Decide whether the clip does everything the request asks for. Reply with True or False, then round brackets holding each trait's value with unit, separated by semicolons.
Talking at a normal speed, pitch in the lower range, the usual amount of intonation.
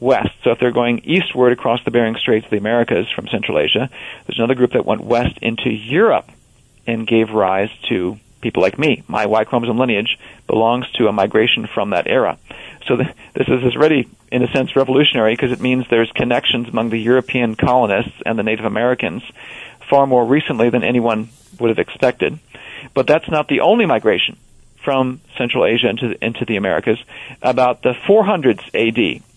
False (185 wpm; 120 Hz; 2.0 semitones)